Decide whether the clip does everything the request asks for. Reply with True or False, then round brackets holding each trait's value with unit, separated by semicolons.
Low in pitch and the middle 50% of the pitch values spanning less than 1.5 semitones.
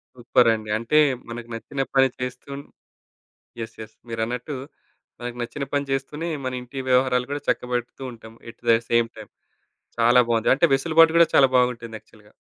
False (125 Hz; 2.7 semitones)